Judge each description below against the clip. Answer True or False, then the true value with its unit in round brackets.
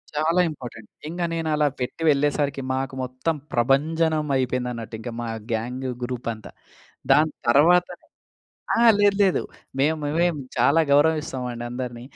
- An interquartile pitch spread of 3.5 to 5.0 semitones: True (4.2 semitones)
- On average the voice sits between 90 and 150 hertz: True (140 Hz)